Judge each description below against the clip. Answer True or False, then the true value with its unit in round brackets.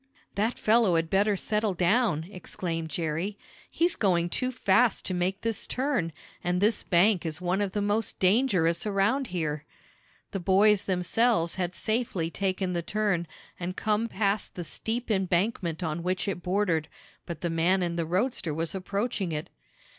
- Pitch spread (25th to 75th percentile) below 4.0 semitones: True (3.6 semitones)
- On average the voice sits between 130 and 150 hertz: False (190 Hz)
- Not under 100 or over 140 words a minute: False (160 wpm)